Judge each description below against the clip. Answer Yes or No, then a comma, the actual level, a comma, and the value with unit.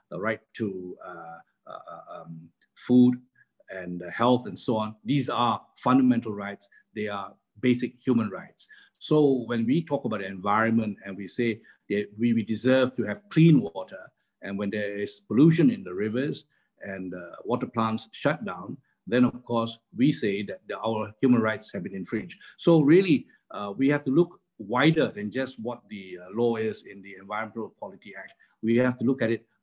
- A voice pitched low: Yes, low, 115 Hz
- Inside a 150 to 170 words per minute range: No, average, 190 wpm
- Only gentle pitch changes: No, average, 3.6 semitones